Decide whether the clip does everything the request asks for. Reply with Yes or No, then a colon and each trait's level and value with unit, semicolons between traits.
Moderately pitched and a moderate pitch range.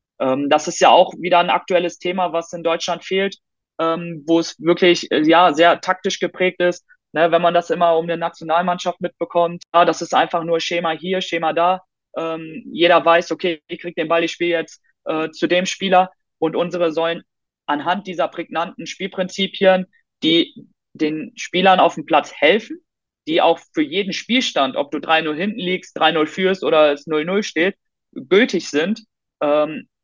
No: medium, 175 Hz; narrow, 2.1 semitones